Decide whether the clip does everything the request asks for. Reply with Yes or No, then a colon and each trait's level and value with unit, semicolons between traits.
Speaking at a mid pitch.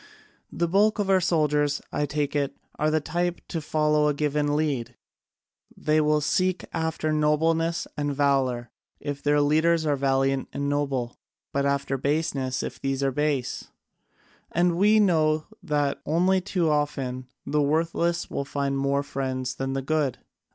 Yes: medium, 150 Hz